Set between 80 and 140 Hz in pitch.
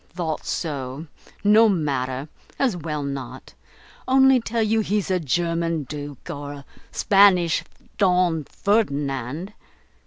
No: medium, 165 Hz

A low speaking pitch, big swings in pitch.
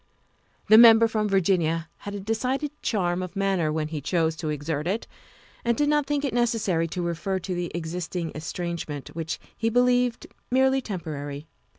No: medium, 185 Hz; wide, 5.8 semitones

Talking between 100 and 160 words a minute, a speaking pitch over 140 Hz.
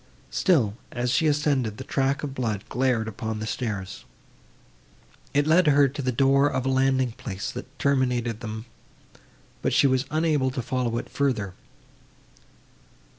No: average, 150 wpm; low, 130 Hz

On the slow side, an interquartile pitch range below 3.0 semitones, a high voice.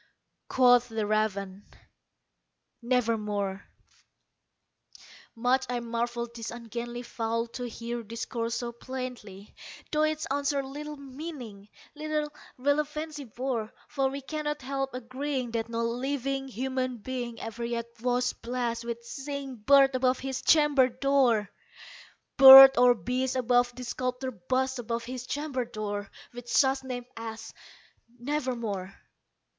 Yes: slow, 120 wpm; narrow, 2.6 semitones; very high, 250 Hz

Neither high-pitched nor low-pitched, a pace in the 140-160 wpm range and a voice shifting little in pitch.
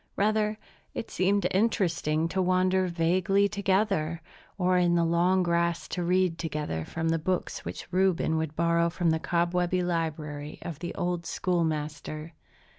Yes: medium, 175 Hz; average, 145 wpm; narrow, 2.2 semitones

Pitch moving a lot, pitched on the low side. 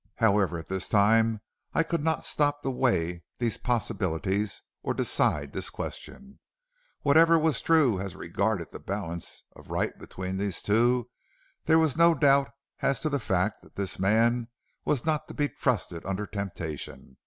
Yes: wide, 7.0 semitones; low, 110 Hz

